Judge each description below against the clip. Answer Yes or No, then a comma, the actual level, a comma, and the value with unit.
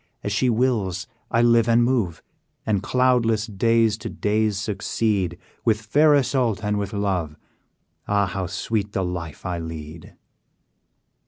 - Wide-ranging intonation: No, average, 3.6 semitones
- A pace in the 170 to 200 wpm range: No, average, 140 wpm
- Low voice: Yes, low, 105 Hz